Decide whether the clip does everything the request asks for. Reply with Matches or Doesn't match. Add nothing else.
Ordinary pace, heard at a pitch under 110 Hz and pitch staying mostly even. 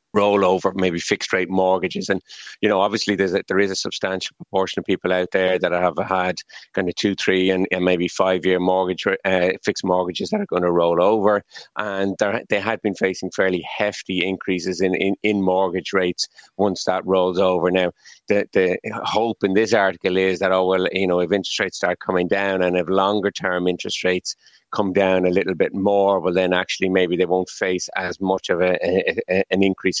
Doesn't match